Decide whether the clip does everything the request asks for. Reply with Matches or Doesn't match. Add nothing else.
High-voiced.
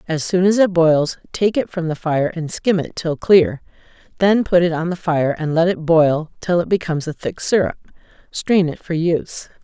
Doesn't match